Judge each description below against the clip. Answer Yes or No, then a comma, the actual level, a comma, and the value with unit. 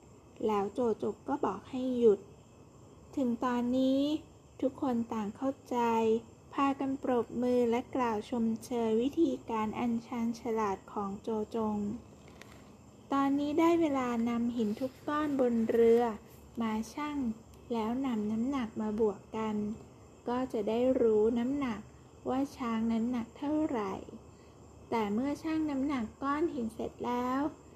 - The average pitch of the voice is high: Yes, high, 240 Hz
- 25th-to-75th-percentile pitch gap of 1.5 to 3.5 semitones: Yes, average, 3.2 semitones